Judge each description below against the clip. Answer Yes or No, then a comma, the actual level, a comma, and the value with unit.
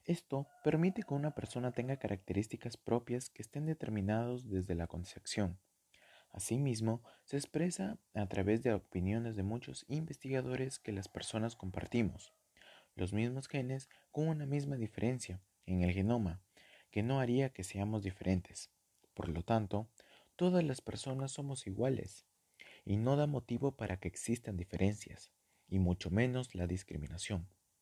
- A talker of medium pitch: No, low, 110 Hz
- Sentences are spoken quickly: No, average, 140 wpm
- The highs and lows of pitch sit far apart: Yes, wide, 5.8 semitones